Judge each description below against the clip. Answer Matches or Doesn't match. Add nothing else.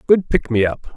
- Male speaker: Matches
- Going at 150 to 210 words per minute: Doesn't match